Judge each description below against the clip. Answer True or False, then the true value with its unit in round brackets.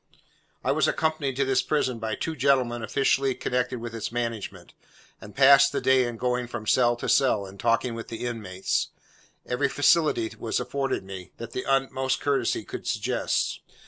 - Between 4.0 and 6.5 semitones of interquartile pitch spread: False (2.9 semitones)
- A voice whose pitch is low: True (125 Hz)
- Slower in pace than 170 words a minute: False (175 wpm)